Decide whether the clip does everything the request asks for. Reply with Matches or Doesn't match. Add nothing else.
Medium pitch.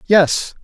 Matches